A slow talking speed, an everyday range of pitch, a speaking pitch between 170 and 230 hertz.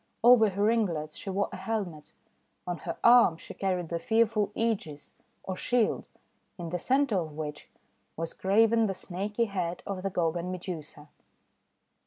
No: average, 165 wpm; average, 4.7 semitones; high, 190 Hz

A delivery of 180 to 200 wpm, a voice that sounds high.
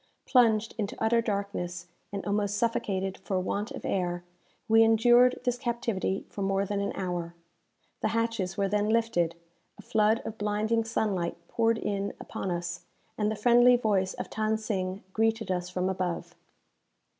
No: average, 155 wpm; high, 210 Hz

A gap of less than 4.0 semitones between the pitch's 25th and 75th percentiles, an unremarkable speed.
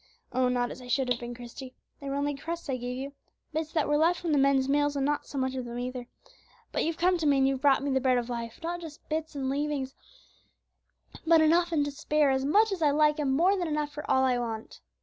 No: average, 3.0 semitones; fast, 265 wpm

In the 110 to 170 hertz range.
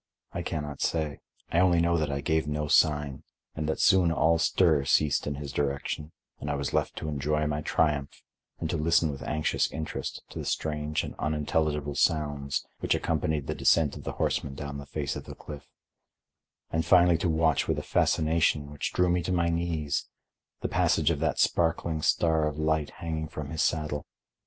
No: very low, 75 Hz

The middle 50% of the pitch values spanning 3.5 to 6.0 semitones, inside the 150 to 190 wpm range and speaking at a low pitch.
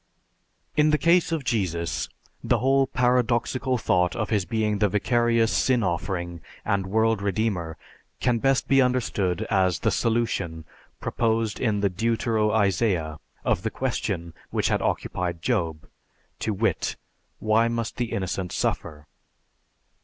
No: average, 4.4 semitones; slow, 135 wpm; low, 110 Hz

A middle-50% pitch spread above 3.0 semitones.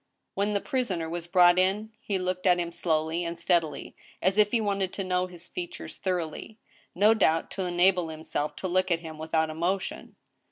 No: narrow, 2.4 semitones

